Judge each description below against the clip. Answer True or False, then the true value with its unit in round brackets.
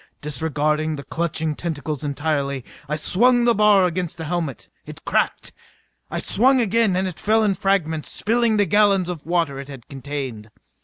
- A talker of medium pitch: True (165 Hz)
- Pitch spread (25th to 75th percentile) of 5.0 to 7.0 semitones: True (5.3 semitones)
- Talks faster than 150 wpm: True (165 wpm)